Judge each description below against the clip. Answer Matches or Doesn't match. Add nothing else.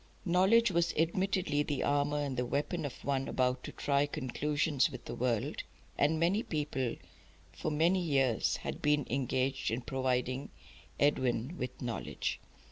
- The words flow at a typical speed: Matches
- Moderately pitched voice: Matches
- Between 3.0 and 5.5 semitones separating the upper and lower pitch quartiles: Matches